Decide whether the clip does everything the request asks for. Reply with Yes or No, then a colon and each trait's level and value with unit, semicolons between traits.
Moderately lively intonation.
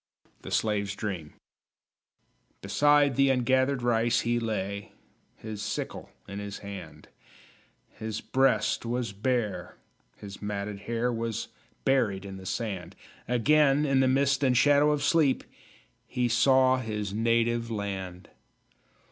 Yes: average, 4.3 semitones